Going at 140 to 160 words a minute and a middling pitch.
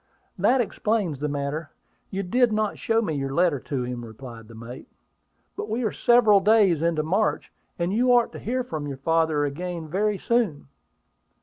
No: average, 180 wpm; medium, 170 Hz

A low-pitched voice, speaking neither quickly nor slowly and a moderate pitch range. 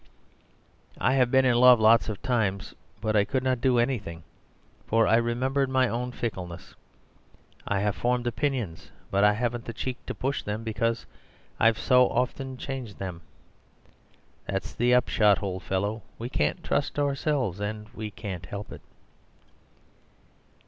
Yes: low, 115 Hz; average, 150 wpm; average, 3.6 semitones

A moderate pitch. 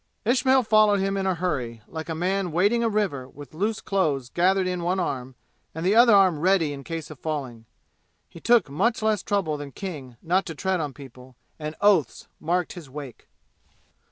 Yes: medium, 175 Hz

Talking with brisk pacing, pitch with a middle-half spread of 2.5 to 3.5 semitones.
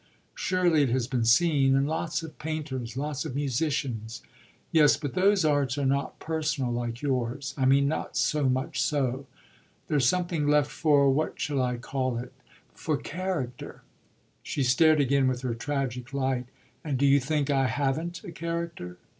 No: average, 165 wpm; average, 3.1 semitones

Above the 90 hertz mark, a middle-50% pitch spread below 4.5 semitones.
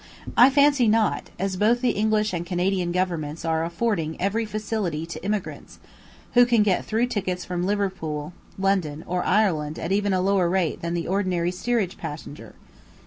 Yes: high, 190 Hz; average, 3.8 semitones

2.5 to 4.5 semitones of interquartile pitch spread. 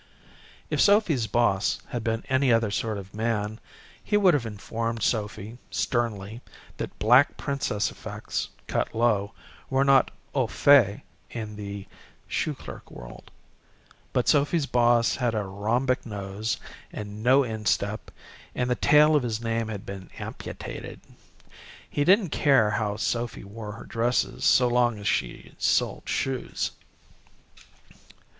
Yes: average, 3.3 semitones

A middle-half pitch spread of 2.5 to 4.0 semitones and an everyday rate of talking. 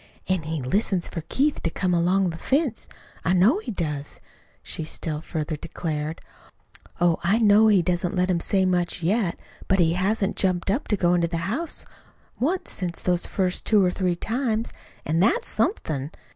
Yes: average, 3.7 semitones; average, 180 wpm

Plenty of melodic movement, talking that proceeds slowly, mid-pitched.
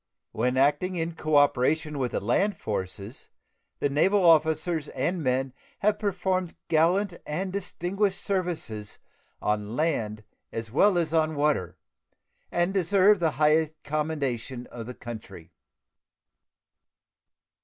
Yes: wide, 6.0 semitones; slow, 115 wpm; medium, 155 Hz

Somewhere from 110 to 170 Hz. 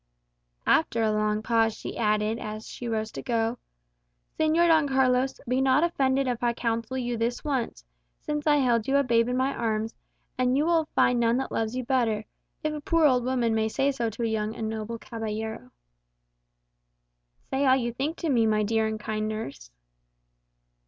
No: high, 235 Hz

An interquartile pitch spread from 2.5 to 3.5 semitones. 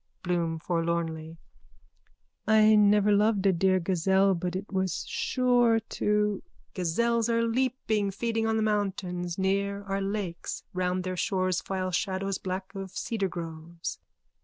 Yes: average, 2.8 semitones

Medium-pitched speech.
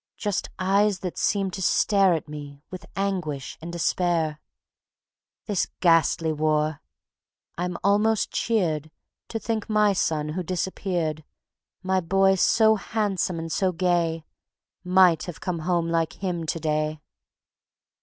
Yes: medium, 180 Hz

